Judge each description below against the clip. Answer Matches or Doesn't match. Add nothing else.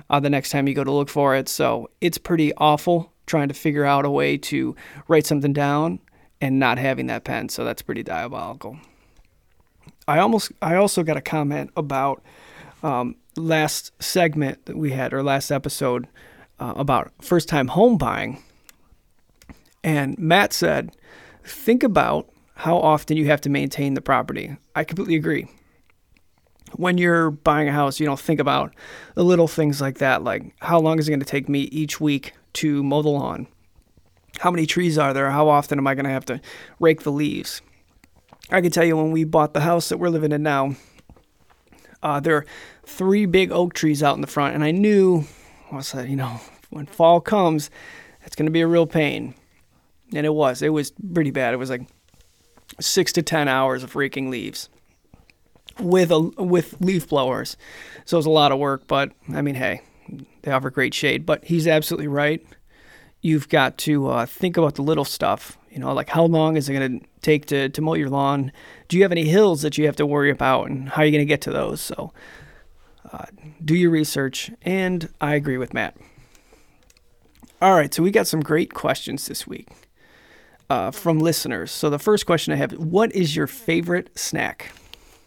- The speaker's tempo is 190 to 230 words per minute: Matches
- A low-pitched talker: Doesn't match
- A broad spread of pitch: Doesn't match